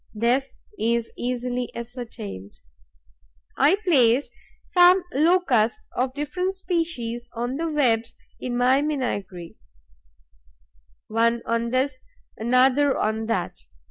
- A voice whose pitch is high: Yes, very high, 250 Hz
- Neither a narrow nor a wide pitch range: Yes, average, 4.0 semitones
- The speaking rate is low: Yes, slow, 100 wpm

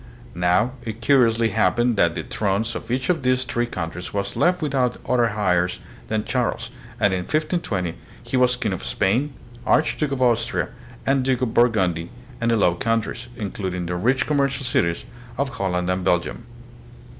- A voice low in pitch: Yes, low, 115 Hz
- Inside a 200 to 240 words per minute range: No, average, 170 wpm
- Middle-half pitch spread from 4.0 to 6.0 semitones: Yes, wide, 5.6 semitones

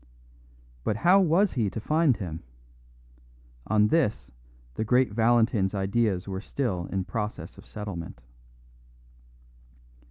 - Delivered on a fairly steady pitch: No, average, 4.5 semitones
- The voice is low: Yes, low, 110 Hz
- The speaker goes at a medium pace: No, slow, 115 wpm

